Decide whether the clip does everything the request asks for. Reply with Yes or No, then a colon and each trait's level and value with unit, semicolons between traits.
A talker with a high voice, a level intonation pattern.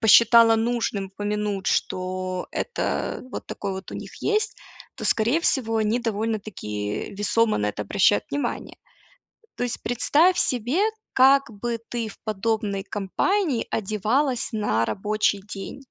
No: high, 220 Hz; average, 3.5 semitones